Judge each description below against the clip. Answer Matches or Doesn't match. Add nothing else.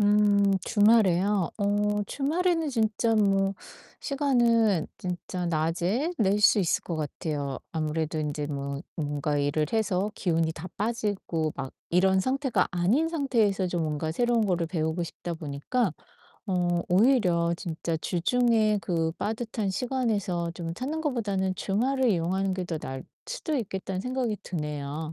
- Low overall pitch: Doesn't match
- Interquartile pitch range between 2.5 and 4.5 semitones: Doesn't match